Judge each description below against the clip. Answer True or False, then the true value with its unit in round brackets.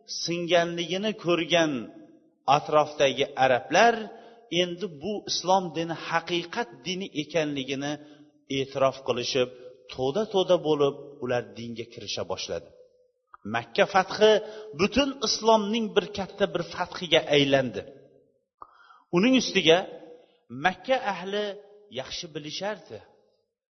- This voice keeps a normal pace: False (90 wpm)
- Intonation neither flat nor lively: False (6.5 semitones)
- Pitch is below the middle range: False (180 Hz)